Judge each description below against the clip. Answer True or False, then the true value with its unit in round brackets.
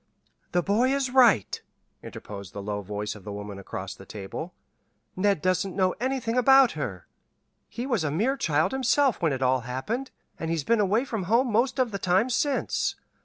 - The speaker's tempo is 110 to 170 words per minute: False (185 wpm)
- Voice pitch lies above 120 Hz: True (190 Hz)